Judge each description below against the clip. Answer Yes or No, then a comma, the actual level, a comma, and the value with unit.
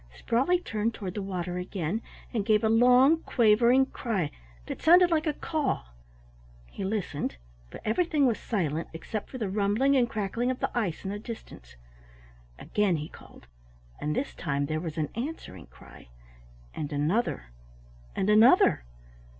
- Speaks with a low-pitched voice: No, high, 215 Hz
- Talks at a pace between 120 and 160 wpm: Yes, average, 155 wpm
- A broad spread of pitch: Yes, wide, 6.2 semitones